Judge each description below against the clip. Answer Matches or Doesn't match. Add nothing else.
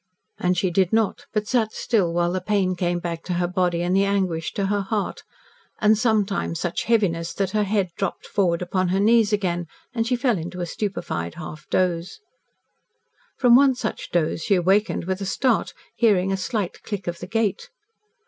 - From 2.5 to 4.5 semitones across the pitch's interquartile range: Matches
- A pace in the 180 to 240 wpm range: Matches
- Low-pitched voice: Doesn't match